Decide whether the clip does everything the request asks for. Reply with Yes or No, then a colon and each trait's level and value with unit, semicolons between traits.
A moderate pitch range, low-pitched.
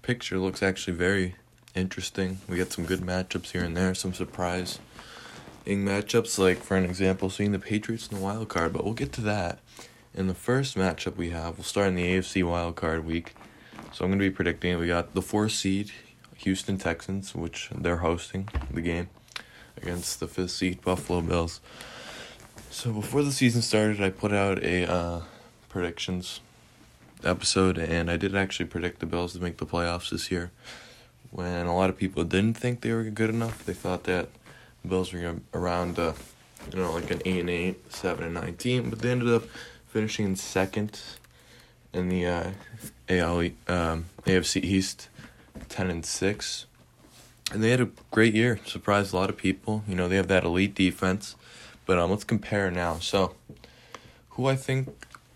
Yes: average, 3.2 semitones; very low, 95 Hz